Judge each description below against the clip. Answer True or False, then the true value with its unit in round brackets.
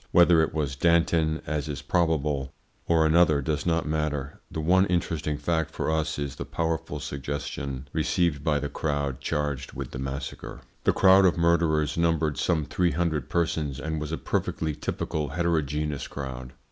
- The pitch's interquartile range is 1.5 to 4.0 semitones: True (2.5 semitones)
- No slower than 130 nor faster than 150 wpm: False (165 wpm)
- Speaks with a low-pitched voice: True (75 Hz)